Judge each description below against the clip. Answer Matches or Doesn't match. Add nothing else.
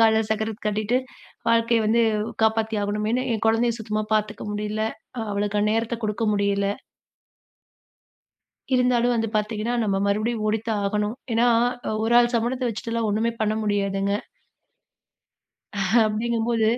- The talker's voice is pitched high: Matches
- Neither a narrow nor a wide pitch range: Doesn't match